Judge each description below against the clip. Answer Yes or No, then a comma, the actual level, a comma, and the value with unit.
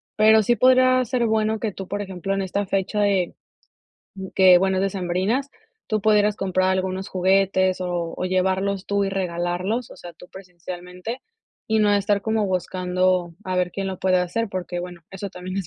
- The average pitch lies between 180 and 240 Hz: Yes, high, 190 Hz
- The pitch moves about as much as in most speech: No, narrow, 2.2 semitones